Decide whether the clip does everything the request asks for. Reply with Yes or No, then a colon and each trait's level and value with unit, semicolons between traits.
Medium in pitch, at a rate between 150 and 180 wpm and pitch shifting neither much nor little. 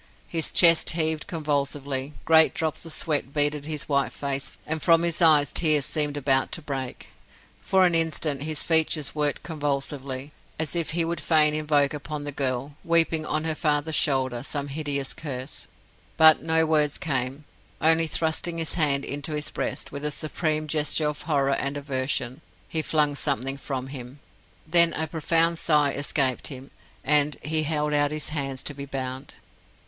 No: medium, 150 Hz; average, 170 wpm; narrow, 2.3 semitones